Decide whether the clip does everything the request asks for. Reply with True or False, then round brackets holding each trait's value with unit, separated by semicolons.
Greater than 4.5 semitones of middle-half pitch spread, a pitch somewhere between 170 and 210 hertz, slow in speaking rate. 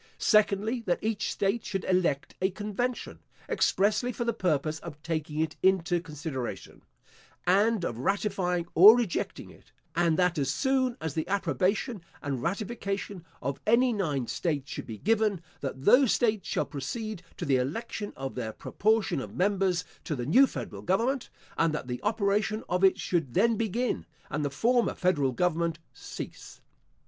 False (5.5 semitones; 185 Hz; 160 wpm)